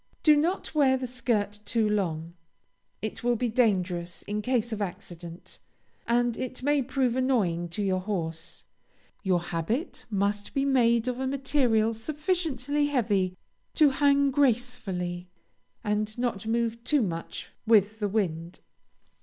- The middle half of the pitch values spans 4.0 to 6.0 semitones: Yes, average, 5.2 semitones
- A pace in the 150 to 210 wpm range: No, slow, 135 wpm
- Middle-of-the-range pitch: No, high, 225 Hz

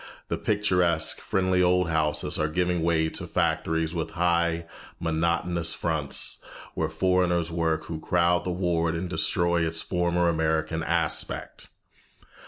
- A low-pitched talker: Yes, very low, 85 Hz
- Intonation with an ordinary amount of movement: No, narrow, 1.5 semitones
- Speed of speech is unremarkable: No, slow, 130 wpm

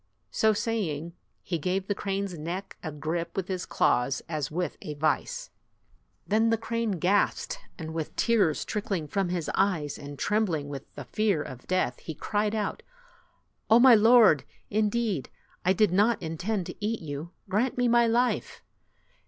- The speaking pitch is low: No, high, 190 Hz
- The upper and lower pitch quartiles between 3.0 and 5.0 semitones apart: No, wide, 5.4 semitones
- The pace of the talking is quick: No, average, 165 wpm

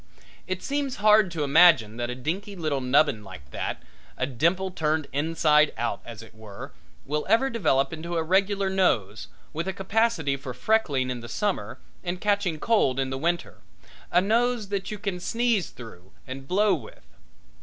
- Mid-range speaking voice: Yes, medium, 165 Hz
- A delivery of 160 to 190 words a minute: Yes, average, 175 wpm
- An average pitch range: No, wide, 7.1 semitones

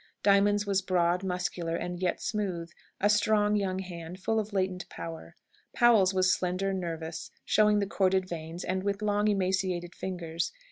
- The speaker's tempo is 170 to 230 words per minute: No, average, 155 wpm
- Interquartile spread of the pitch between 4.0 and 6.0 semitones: No, narrow, 2.5 semitones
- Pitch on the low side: No, medium, 185 Hz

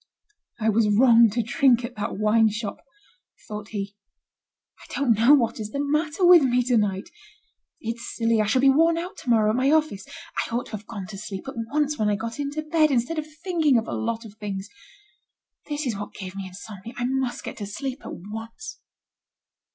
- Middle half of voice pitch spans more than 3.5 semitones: Yes, average, 5.0 semitones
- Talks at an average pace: No, fast, 210 wpm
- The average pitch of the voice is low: No, high, 230 Hz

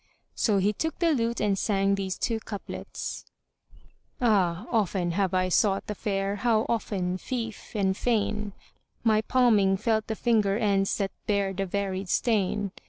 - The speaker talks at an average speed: Yes, average, 160 wpm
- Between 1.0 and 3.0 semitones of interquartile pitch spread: Yes, narrow, 2.4 semitones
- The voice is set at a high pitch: Yes, high, 205 Hz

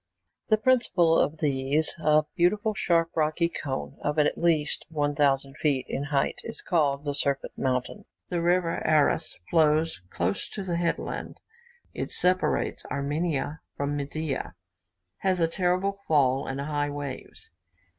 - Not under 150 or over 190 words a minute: No, slow, 135 wpm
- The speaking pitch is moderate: Yes, medium, 155 Hz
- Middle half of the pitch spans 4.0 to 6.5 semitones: No, average, 3.3 semitones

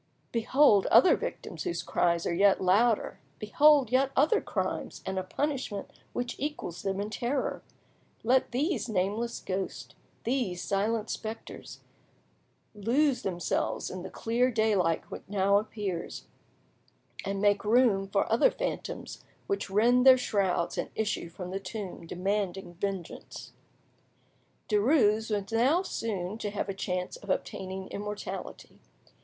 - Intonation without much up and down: No, average, 4.2 semitones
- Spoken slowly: Yes, slow, 130 wpm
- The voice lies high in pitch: Yes, high, 210 Hz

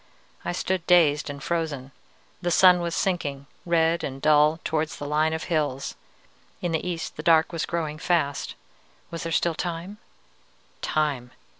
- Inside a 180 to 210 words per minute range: No, average, 155 wpm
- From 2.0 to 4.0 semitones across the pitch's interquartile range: Yes, narrow, 2.5 semitones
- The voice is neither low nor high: Yes, medium, 160 Hz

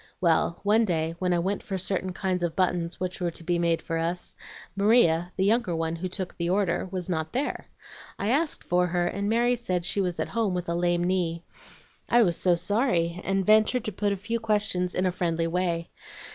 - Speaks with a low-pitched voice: No, medium, 180 Hz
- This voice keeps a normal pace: No, fast, 215 wpm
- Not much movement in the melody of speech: No, average, 3.0 semitones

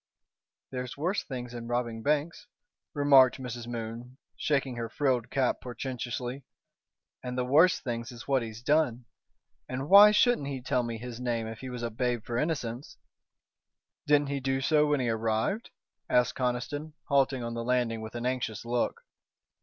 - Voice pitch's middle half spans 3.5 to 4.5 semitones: No, average, 3.0 semitones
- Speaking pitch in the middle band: No, low, 125 Hz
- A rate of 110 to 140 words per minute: No, average, 165 wpm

